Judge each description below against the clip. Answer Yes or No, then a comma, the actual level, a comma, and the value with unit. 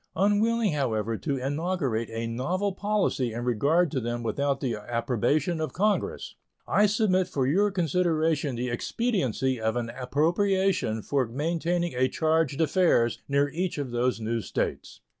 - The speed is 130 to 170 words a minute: Yes, average, 145 wpm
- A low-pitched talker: No, medium, 145 Hz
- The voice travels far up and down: Yes, wide, 6.9 semitones